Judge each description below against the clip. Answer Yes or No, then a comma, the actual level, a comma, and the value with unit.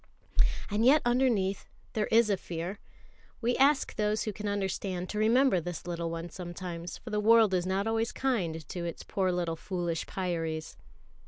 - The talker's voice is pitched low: No, high, 190 Hz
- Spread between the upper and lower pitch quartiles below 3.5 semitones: No, average, 4.2 semitones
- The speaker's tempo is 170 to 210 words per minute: Yes, average, 175 wpm